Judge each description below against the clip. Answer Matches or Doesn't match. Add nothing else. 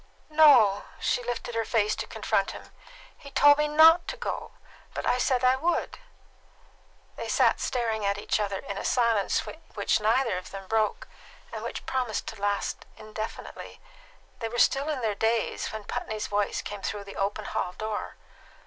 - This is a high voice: Matches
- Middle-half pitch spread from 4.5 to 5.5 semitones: Doesn't match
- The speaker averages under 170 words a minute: Doesn't match